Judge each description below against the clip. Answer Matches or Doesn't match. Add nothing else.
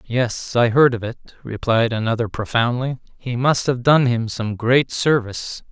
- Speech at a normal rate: Matches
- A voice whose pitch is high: Doesn't match